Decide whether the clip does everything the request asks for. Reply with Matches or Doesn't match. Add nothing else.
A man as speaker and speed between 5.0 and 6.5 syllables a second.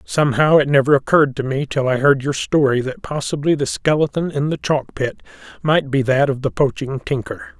Matches